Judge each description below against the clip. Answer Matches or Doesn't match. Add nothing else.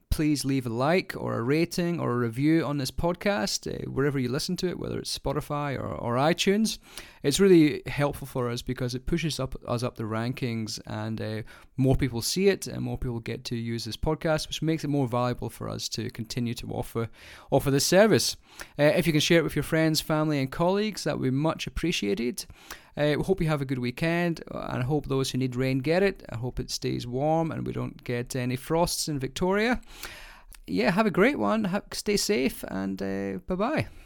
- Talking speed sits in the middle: Doesn't match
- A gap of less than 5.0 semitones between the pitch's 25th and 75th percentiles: Doesn't match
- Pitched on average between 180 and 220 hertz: Doesn't match